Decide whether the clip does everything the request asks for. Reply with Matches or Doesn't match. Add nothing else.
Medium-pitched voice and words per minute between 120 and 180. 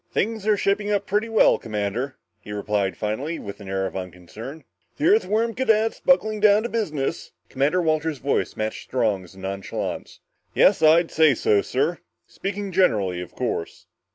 Matches